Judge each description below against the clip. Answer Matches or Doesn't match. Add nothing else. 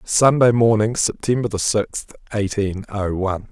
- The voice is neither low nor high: Doesn't match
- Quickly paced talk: Doesn't match